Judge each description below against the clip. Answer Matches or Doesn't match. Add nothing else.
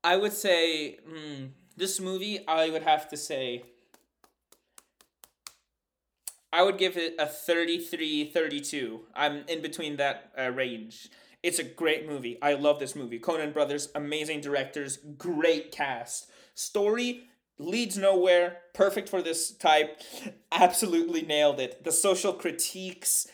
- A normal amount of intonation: Matches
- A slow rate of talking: Matches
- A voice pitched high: Doesn't match